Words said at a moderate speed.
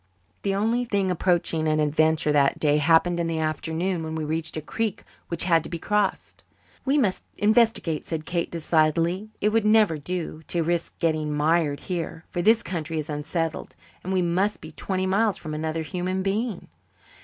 Yes: average, 180 wpm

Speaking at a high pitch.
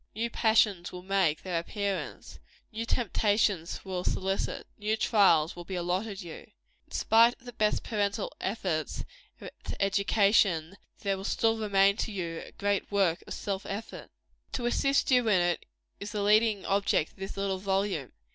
Yes: high, 200 Hz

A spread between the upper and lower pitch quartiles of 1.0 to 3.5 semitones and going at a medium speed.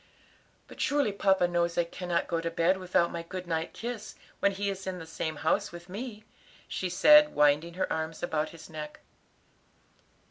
Yes: average, 2.8 semitones; average, 180 wpm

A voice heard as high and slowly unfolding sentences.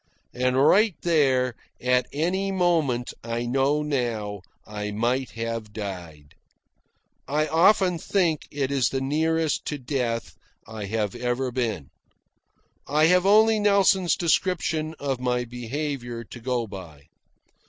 No: low, 130 Hz; slow, 125 wpm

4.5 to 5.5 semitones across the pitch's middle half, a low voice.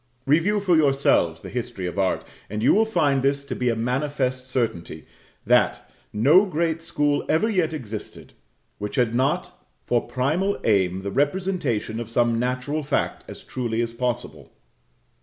Yes: average, 5.1 semitones; low, 130 Hz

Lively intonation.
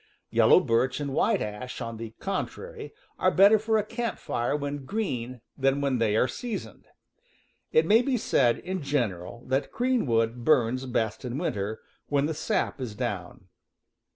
Yes: wide, 9.0 semitones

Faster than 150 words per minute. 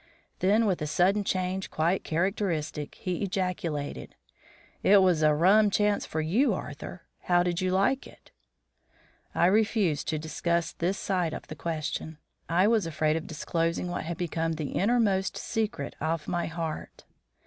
Yes: average, 160 wpm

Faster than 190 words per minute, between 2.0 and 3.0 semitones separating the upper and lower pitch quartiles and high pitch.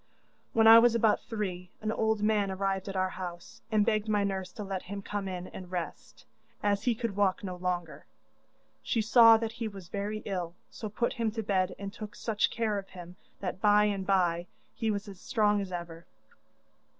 Yes: average, 200 wpm; average, 2.7 semitones; high, 200 Hz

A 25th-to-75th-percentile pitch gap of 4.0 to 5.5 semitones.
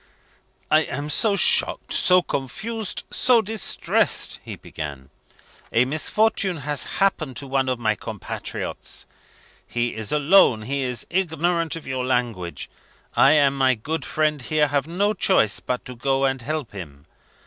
Yes: average, 5.1 semitones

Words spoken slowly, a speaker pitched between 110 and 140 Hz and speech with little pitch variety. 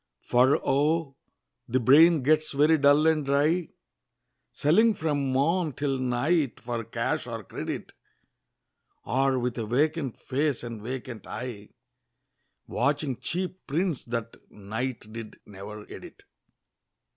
No: slow, 120 wpm; low, 135 Hz; average, 4.2 semitones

